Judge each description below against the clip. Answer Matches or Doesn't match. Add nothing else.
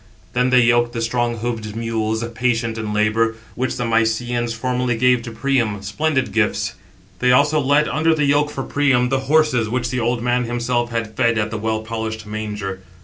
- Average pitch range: Doesn't match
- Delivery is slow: Doesn't match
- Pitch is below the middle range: Matches